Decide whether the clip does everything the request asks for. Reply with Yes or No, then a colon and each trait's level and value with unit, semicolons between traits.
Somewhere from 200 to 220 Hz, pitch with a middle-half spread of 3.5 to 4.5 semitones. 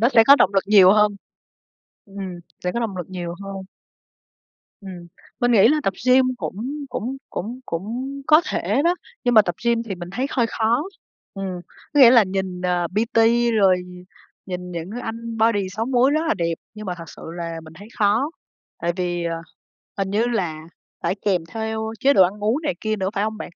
Yes: high, 205 Hz; average, 4.2 semitones